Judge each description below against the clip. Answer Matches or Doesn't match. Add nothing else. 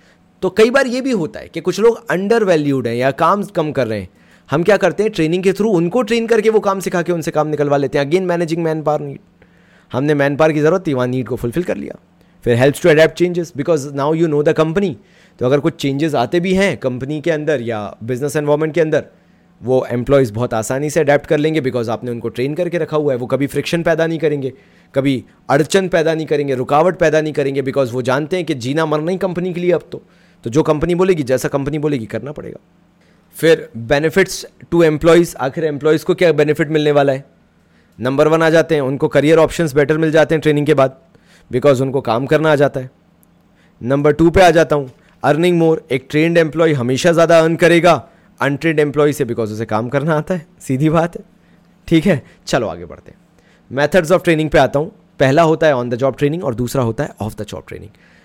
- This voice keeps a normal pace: Doesn't match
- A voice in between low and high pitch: Matches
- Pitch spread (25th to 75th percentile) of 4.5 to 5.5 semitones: Doesn't match